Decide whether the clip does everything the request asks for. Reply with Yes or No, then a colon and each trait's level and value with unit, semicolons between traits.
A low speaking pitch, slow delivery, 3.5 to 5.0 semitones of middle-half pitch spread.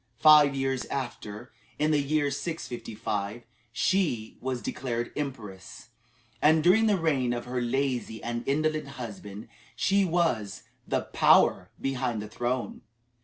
Yes: low, 130 Hz; slow, 125 wpm; average, 4.4 semitones